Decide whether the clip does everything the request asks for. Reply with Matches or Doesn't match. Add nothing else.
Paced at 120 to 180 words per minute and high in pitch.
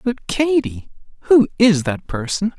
Matches